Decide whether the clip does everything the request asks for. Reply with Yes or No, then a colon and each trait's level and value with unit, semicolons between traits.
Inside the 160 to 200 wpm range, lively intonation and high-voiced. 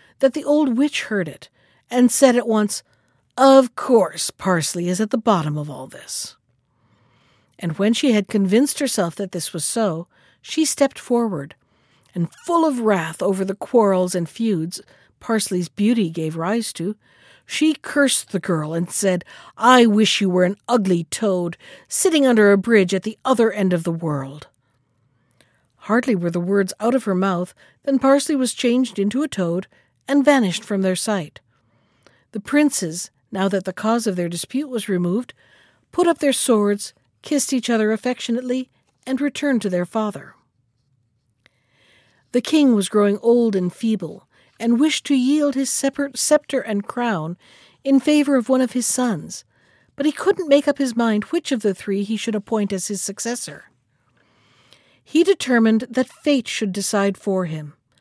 Yes: average, 170 wpm; wide, 6.5 semitones; high, 210 Hz